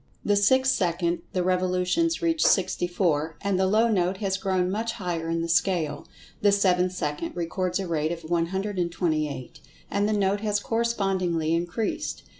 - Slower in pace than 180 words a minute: Yes, average, 160 wpm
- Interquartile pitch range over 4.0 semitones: No, average, 3.0 semitones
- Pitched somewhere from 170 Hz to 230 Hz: Yes, medium, 185 Hz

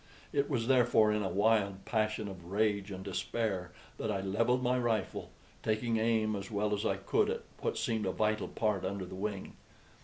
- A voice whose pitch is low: Yes, low, 105 Hz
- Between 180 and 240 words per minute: Yes, average, 190 wpm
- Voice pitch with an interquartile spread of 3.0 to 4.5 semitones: No, narrow, 2.4 semitones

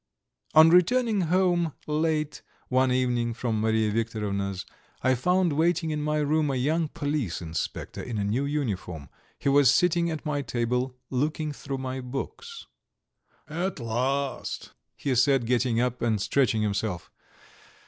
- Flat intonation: No, average, 4.9 semitones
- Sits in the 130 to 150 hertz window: Yes, low, 135 Hz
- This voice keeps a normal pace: Yes, average, 145 wpm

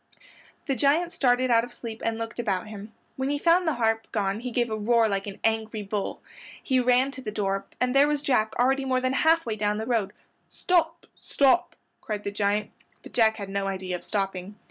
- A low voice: No, high, 230 Hz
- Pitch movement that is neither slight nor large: Yes, average, 4.1 semitones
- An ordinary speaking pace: No, fast, 215 wpm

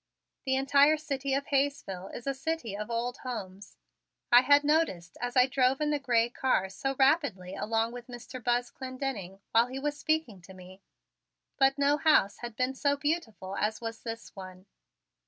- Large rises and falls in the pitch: No, average, 4.4 semitones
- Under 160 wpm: No, average, 175 wpm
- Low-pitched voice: No, very high, 250 Hz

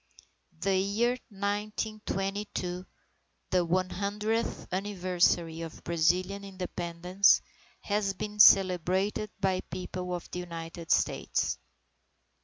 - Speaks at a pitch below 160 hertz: No, medium, 185 Hz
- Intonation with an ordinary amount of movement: No, narrow, 2.2 semitones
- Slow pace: Yes, slow, 90 wpm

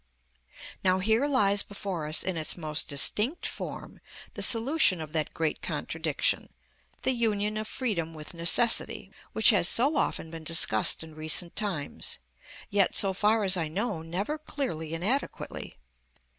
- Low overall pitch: No, high, 190 Hz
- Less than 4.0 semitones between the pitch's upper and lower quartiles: No, average, 5.3 semitones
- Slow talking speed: No, average, 150 wpm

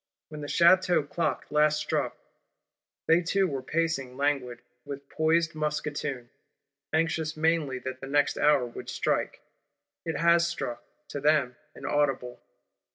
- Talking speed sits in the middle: No, slow, 130 wpm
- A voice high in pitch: No, medium, 150 Hz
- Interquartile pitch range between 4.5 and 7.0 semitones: No, average, 3.2 semitones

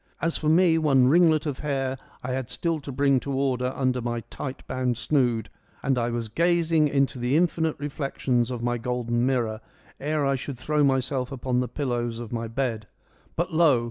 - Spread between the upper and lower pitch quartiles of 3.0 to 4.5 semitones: Yes, average, 3.4 semitones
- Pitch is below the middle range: Yes, low, 130 Hz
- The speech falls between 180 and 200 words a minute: Yes, average, 190 wpm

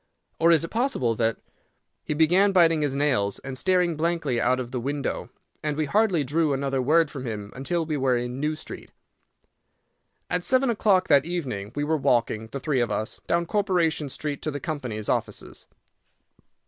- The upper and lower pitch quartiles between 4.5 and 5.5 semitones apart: Yes, average, 4.8 semitones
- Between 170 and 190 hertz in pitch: No, medium, 150 Hz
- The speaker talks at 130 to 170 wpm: No, average, 180 wpm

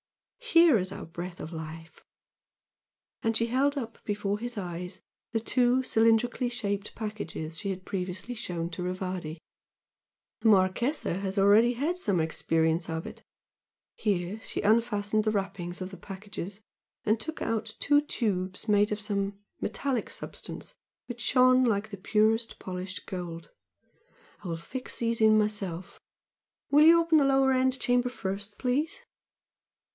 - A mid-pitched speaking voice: No, high, 210 Hz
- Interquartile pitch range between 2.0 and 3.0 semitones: No, average, 4.7 semitones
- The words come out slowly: No, average, 145 wpm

